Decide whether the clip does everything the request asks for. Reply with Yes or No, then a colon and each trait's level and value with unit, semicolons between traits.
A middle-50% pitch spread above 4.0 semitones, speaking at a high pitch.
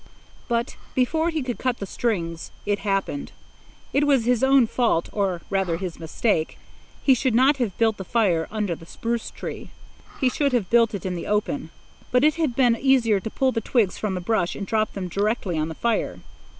Yes: average, 4.7 semitones; high, 225 Hz